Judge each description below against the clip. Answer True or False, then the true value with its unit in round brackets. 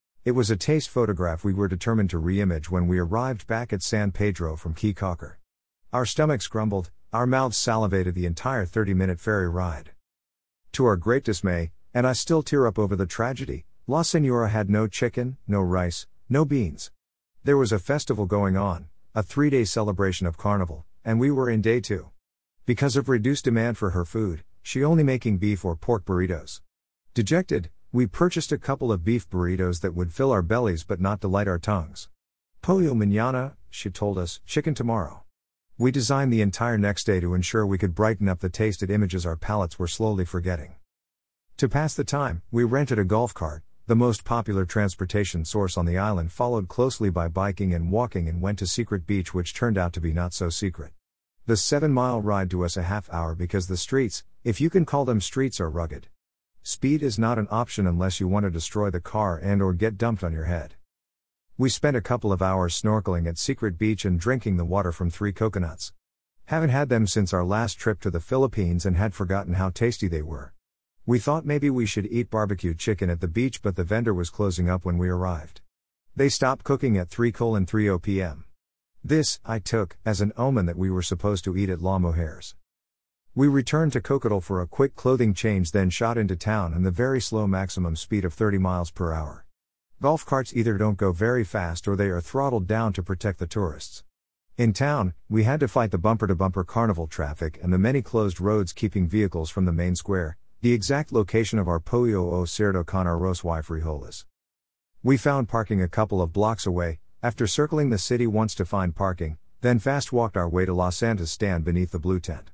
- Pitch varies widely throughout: False (4.8 semitones)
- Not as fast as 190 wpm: False (205 wpm)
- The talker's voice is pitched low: True (100 Hz)